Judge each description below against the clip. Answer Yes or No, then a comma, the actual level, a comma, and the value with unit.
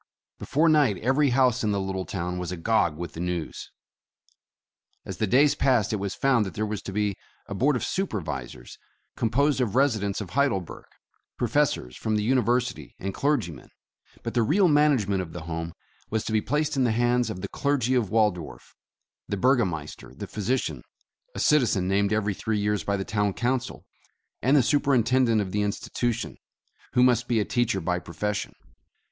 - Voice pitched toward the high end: No, low, 110 Hz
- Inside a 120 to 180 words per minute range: No, average, 190 wpm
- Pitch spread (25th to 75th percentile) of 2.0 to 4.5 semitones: No, average, 4.9 semitones